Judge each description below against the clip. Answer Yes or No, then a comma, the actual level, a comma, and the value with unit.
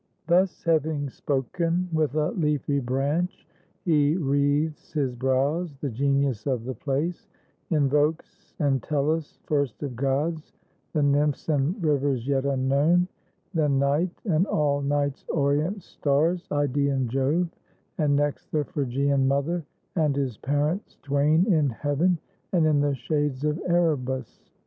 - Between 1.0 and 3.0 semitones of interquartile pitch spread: Yes, narrow, 2.5 semitones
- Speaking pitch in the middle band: Yes, medium, 145 Hz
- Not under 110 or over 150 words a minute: Yes, slow, 135 wpm